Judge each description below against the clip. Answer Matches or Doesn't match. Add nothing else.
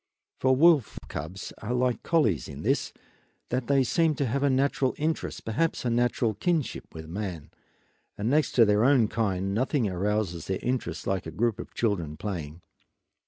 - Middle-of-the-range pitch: Doesn't match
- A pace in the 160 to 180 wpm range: Matches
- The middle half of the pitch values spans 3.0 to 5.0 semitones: Doesn't match